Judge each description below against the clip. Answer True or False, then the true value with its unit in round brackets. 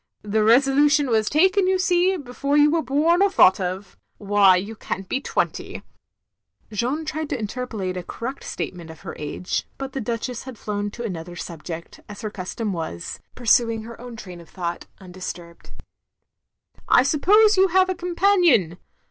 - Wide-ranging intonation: True (7.9 semitones)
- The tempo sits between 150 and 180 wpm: True (170 wpm)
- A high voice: True (230 Hz)